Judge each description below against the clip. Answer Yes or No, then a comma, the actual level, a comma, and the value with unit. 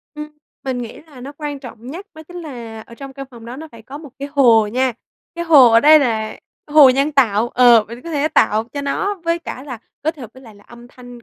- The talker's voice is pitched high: Yes, very high, 260 Hz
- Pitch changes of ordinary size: Yes, average, 3.9 semitones